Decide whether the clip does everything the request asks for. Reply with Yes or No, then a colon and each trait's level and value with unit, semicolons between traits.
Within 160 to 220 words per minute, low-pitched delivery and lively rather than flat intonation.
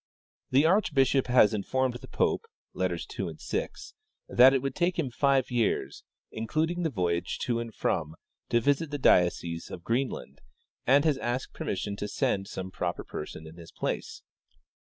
Yes: average, 165 wpm; low, 120 Hz; wide, 6.7 semitones